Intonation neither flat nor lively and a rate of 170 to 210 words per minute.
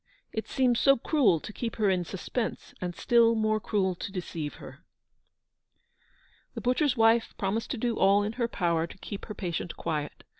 Yes: average, 4.5 semitones; average, 180 wpm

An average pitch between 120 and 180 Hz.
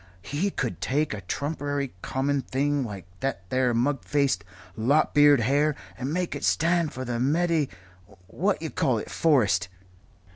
Yes: medium, 140 Hz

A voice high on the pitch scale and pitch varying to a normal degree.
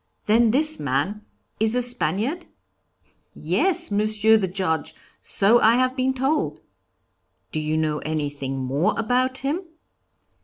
No: high, 215 Hz; wide, 8.3 semitones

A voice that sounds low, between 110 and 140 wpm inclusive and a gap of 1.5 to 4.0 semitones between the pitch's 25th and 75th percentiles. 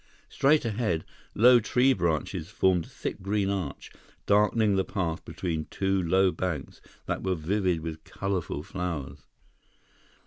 Yes: very low, 95 Hz; slow, 135 wpm; average, 3.7 semitones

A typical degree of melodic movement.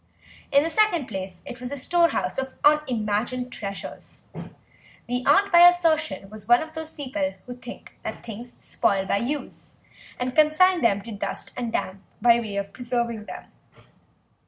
No: wide, 6.2 semitones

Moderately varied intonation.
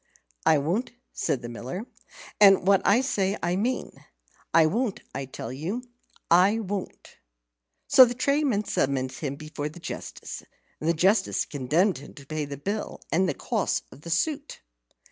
No: wide, 6.5 semitones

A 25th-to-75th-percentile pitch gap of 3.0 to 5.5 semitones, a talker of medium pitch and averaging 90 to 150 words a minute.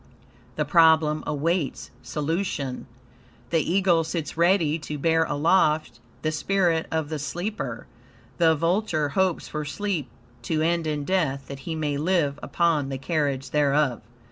No: narrow, 2.6 semitones; medium, 160 Hz; average, 140 wpm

